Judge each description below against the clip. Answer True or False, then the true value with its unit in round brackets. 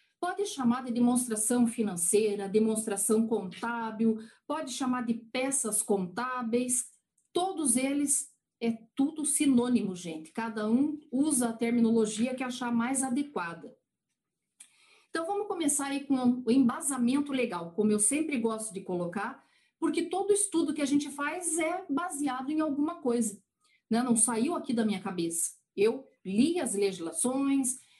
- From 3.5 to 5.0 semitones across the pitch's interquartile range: True (4.5 semitones)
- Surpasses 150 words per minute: False (135 wpm)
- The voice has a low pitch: False (245 Hz)